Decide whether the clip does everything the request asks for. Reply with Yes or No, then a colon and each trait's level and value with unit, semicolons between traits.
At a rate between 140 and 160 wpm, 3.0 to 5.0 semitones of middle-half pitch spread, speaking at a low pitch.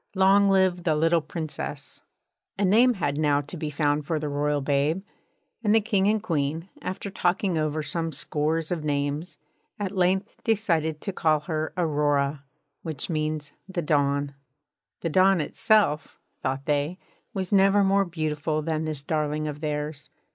No: average, 155 wpm; average, 4.2 semitones; medium, 155 Hz